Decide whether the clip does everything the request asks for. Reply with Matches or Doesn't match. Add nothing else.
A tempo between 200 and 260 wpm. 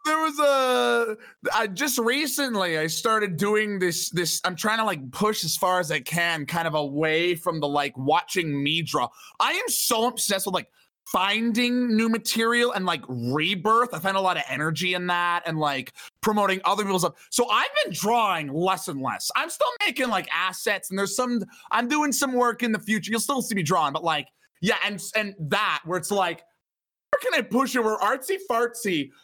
Matches